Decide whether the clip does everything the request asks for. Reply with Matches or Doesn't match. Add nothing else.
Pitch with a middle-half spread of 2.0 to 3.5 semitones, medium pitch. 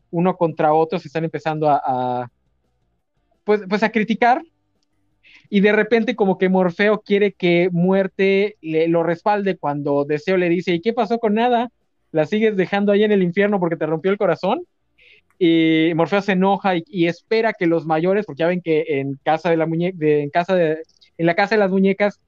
Doesn't match